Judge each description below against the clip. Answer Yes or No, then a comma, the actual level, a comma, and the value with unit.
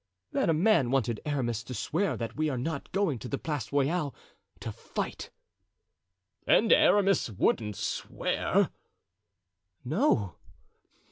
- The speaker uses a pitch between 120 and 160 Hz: Yes, medium, 140 Hz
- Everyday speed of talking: No, slow, 120 wpm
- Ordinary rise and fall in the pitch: No, wide, 6.1 semitones